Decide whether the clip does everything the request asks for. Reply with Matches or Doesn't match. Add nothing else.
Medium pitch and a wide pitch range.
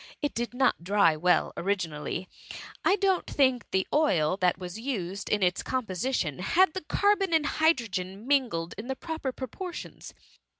Doesn't match